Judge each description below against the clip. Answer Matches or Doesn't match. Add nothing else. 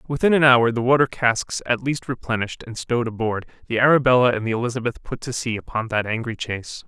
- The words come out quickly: Matches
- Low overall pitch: Matches